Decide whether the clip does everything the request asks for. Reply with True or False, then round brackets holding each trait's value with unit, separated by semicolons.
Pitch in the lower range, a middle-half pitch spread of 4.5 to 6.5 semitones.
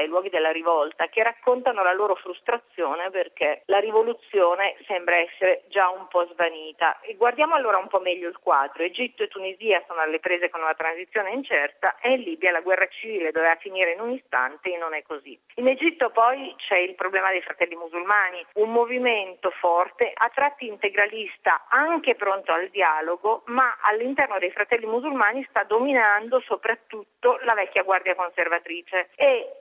False (195 Hz; 5.4 semitones)